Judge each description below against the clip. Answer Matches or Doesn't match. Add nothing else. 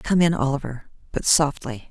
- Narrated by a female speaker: Matches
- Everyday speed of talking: Matches